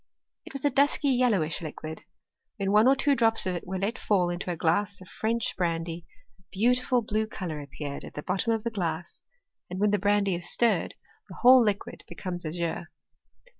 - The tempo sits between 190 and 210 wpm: Yes, average, 200 wpm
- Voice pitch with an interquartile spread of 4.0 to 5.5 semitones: Yes, average, 5.0 semitones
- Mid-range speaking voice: No, high, 200 Hz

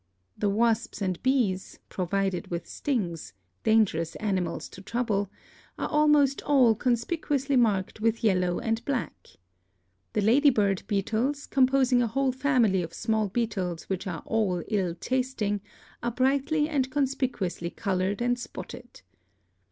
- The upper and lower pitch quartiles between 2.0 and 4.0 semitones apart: No, average, 5.2 semitones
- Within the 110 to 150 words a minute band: Yes, slow, 135 wpm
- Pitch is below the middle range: No, high, 225 Hz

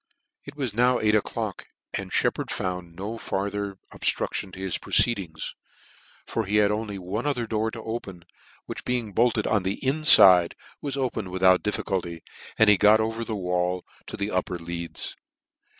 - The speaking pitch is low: Yes, low, 100 Hz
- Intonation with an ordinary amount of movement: Yes, average, 3.5 semitones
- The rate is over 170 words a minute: No, average, 165 wpm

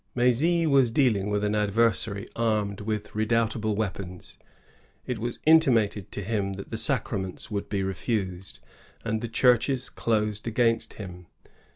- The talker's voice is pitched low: Yes, low, 110 Hz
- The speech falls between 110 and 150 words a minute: Yes, average, 145 wpm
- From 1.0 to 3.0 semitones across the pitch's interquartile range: Yes, average, 2.7 semitones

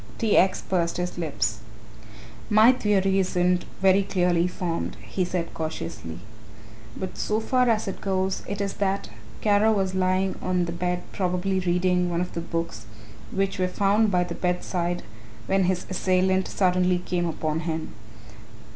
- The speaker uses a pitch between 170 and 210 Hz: Yes, medium, 185 Hz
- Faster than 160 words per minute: No, average, 155 wpm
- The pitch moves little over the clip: Yes, narrow, 1.7 semitones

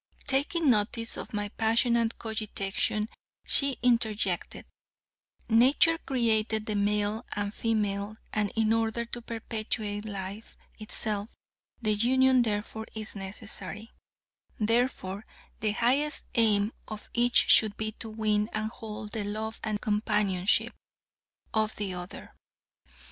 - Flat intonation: Yes, narrow, 1.8 semitones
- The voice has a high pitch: Yes, high, 215 Hz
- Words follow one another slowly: Yes, slow, 115 wpm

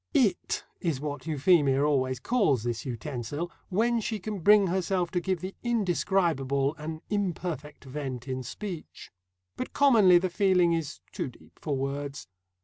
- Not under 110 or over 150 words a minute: Yes, average, 145 wpm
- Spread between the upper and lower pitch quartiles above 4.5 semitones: Yes, wide, 5.5 semitones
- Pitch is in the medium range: Yes, medium, 165 Hz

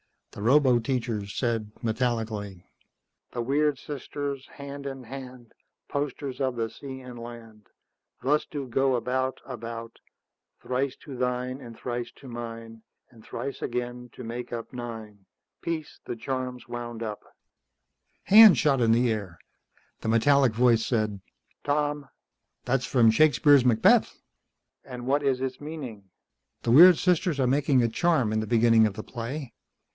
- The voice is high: No, low, 125 Hz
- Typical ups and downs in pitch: Yes, average, 3.1 semitones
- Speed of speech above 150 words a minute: No, average, 145 wpm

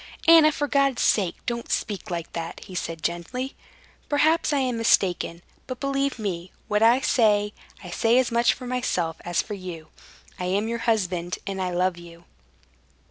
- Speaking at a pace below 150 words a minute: No, average, 175 wpm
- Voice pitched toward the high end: Yes, high, 210 Hz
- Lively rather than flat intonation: Yes, wide, 6.2 semitones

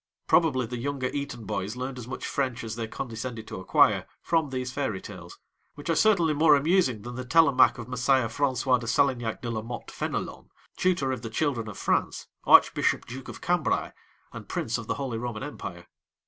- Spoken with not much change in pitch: No, average, 3.7 semitones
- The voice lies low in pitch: Yes, low, 125 Hz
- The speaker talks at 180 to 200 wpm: Yes, average, 190 wpm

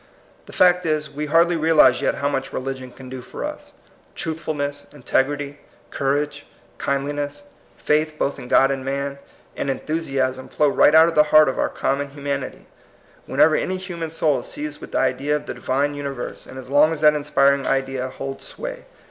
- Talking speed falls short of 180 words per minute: No, average, 190 wpm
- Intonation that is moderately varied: No, narrow, 2.2 semitones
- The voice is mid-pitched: Yes, medium, 145 Hz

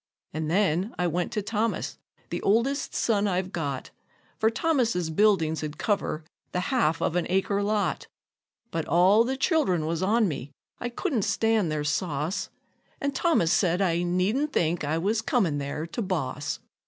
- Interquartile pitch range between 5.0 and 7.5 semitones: Yes, wide, 5.5 semitones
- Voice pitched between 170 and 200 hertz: Yes, medium, 185 Hz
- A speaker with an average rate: Yes, average, 165 wpm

